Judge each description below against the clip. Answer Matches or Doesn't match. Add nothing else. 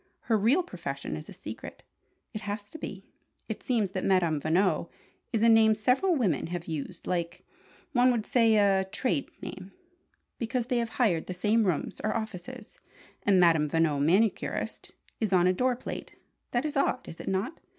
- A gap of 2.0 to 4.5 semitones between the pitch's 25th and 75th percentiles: Doesn't match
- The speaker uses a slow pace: Doesn't match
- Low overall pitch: Doesn't match